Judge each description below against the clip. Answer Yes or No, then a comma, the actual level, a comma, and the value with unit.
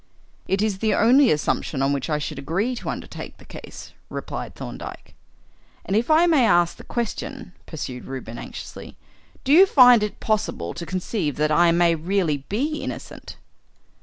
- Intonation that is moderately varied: No, wide, 7.6 semitones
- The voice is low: No, high, 190 Hz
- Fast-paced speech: No, average, 170 wpm